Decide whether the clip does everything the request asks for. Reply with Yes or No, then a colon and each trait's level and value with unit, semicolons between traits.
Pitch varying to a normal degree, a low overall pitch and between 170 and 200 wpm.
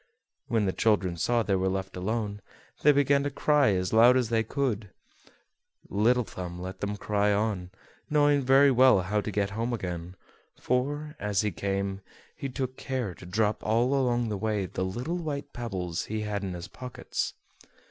Yes: average, 4.7 semitones; low, 110 Hz; average, 180 wpm